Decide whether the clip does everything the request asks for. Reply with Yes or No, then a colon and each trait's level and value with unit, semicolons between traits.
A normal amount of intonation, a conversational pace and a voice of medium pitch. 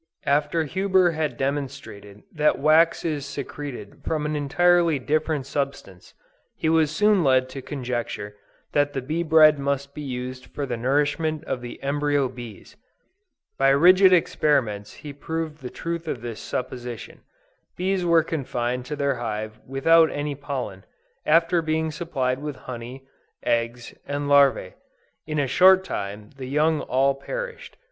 Yes: average, 3.8 semitones; average, 145 wpm; medium, 145 Hz